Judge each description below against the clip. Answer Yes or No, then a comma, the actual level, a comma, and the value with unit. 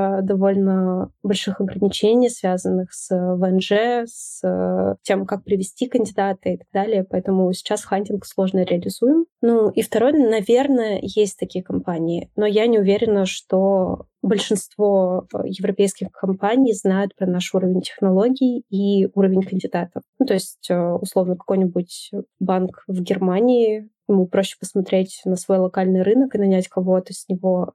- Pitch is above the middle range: Yes, high, 195 Hz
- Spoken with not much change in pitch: Yes, narrow, 2.2 semitones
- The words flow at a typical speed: Yes, average, 135 wpm